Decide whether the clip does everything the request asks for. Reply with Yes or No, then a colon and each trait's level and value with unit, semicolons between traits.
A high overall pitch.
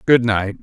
No: low, 110 Hz